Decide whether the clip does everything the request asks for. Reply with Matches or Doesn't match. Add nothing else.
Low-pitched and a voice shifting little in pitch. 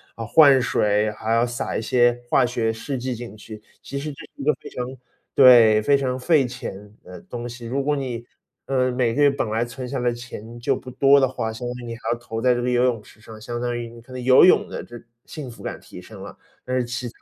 Matches